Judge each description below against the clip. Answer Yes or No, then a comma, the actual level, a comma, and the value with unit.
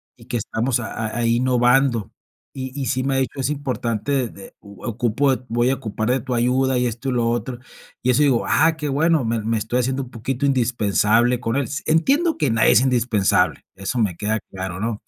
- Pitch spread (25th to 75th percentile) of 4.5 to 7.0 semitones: No, average, 2.8 semitones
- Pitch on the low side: Yes, low, 125 Hz